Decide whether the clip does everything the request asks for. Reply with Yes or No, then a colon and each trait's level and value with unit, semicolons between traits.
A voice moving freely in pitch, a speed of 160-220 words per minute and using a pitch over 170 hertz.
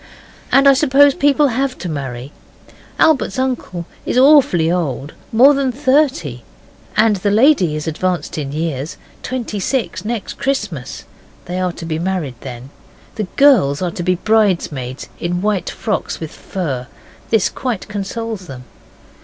No: wide, 8.2 semitones; average, 145 wpm; high, 190 Hz